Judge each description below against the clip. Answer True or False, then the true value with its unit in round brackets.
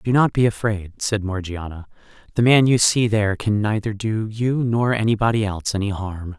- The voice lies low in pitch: True (105 Hz)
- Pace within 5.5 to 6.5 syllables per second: False (5.1 syllables/s)